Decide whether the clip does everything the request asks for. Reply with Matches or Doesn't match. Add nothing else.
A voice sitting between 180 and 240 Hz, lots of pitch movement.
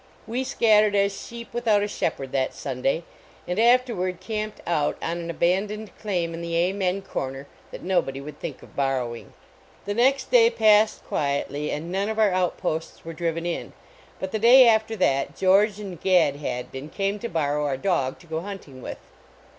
Matches